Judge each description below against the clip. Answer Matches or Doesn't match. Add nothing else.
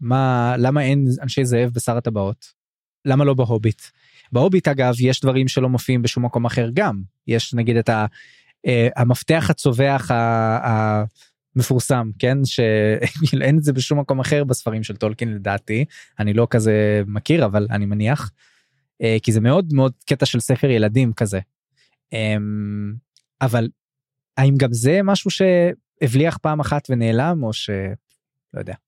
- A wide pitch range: Doesn't match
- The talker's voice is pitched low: Matches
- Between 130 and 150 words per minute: Matches